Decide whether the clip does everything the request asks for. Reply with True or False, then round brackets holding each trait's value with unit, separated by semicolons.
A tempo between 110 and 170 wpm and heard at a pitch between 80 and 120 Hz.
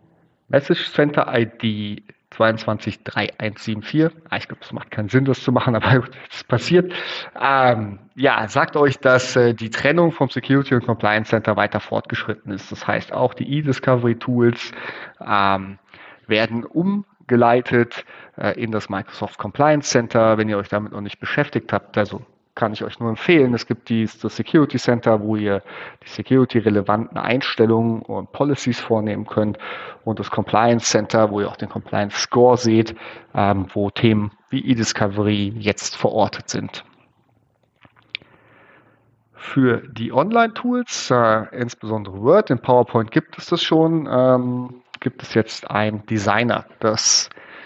True (135 wpm; 115 Hz)